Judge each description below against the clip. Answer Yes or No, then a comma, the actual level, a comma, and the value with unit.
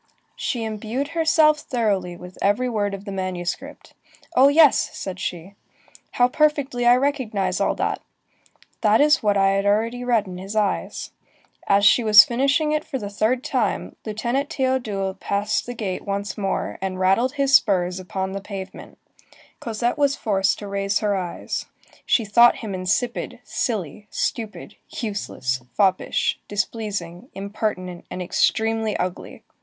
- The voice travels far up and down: No, average, 4.1 semitones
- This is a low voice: No, high, 210 Hz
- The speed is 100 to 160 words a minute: Yes, average, 150 wpm